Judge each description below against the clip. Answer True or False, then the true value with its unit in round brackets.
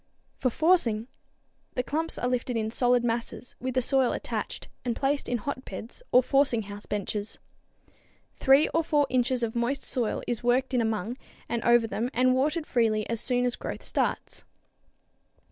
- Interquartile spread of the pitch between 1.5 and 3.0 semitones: True (2.5 semitones)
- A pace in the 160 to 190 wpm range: True (165 wpm)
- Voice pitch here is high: True (245 Hz)